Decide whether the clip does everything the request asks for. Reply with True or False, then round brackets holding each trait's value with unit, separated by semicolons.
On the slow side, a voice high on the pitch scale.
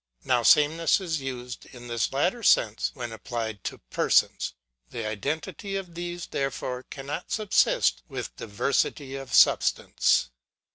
False (130 wpm; 135 Hz)